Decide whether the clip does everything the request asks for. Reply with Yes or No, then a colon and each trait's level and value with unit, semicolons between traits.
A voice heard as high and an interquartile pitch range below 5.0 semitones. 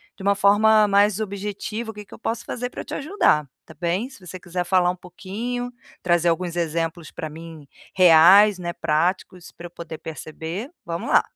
No: medium, 180 Hz; average, 3.8 semitones